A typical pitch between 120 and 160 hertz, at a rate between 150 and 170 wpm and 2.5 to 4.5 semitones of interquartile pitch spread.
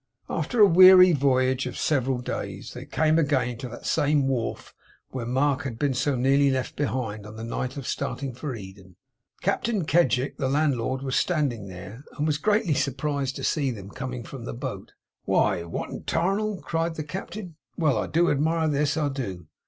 No: medium, 140 Hz; average, 190 wpm; average, 4.0 semitones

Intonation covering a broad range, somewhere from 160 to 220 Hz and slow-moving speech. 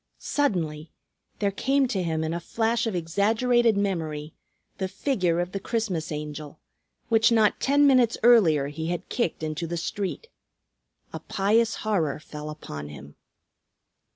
No: wide, 6.3 semitones; medium, 185 Hz; average, 145 wpm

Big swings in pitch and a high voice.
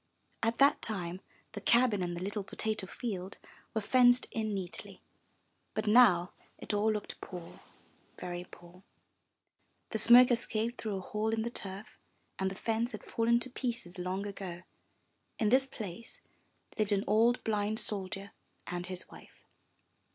No: average, 3.4 semitones; high, 210 Hz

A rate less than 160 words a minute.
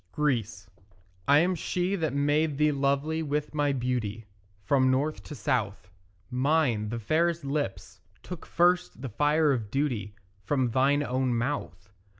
Yes: average, 145 wpm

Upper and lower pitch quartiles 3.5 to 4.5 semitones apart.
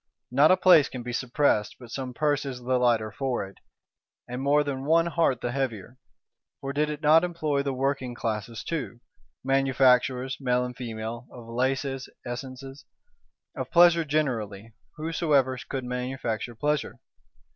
No: average, 3.0 semitones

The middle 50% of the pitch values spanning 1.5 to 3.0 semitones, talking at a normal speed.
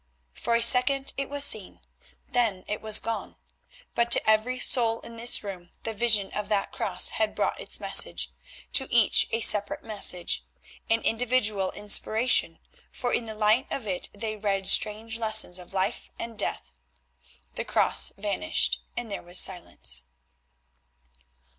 Yes: average, 2.7 semitones; average, 155 wpm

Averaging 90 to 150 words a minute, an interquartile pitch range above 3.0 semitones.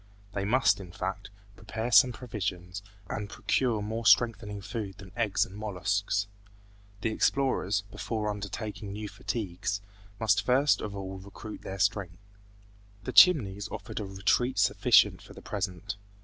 No: average, 140 wpm; narrow, 2.4 semitones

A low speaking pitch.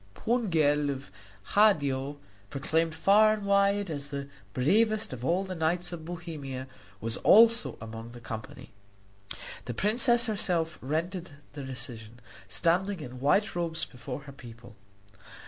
No: medium, 160 Hz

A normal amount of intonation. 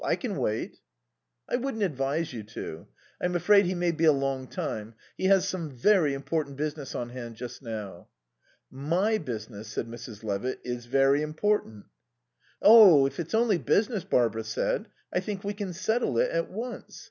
No: wide, 8.3 semitones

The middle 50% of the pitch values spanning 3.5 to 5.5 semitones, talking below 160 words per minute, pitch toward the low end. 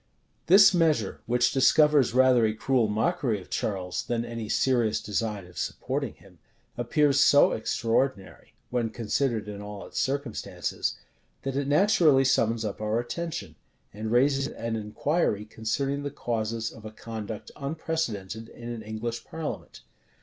Yes: average, 4.2 semitones; average, 140 wpm; low, 115 Hz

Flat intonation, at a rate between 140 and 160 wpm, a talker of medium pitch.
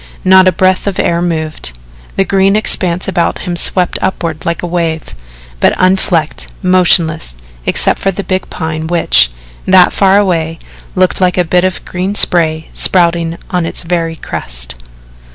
Yes: narrow, 2.3 semitones; average, 155 wpm; medium, 175 Hz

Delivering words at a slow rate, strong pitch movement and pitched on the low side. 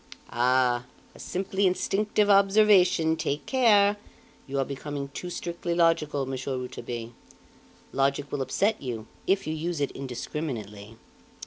No: slow, 125 wpm; wide, 6.4 semitones; medium, 150 Hz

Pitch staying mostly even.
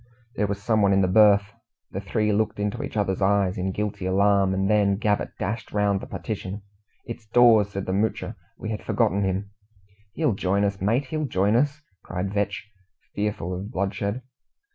Yes: narrow, 1.6 semitones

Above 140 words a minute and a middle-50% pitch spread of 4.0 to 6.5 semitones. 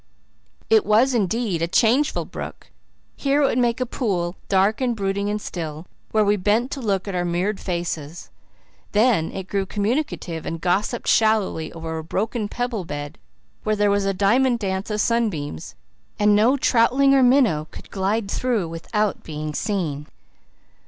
Yes: average, 165 wpm; average, 4.9 semitones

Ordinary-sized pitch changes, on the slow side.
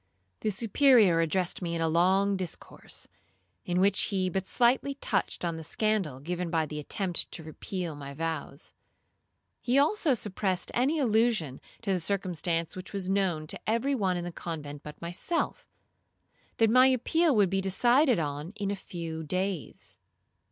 No: average, 4.8 semitones; average, 160 wpm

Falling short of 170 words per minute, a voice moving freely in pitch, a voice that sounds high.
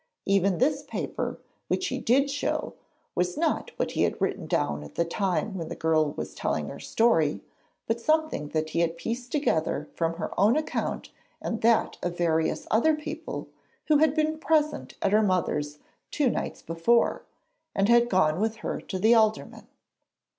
No: average, 175 wpm; wide, 8.3 semitones; high, 215 Hz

